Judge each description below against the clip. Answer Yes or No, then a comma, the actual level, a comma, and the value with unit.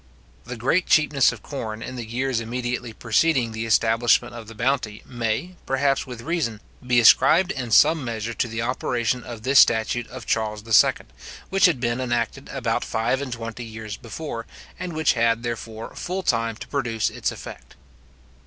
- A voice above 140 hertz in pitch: No, low, 120 Hz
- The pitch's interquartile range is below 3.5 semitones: Yes, average, 2.8 semitones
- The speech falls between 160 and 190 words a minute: Yes, average, 170 wpm